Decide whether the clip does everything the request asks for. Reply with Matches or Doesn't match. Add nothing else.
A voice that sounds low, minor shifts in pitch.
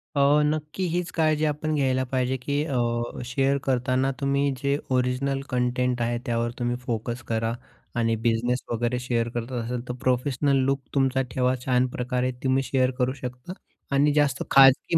Matches